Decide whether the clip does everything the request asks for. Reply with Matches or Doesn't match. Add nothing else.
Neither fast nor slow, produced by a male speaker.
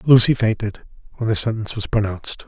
Matches